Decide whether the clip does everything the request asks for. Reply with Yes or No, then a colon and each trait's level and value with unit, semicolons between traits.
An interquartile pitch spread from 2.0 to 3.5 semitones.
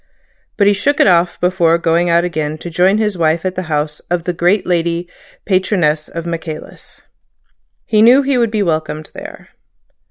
Yes: average, 3.0 semitones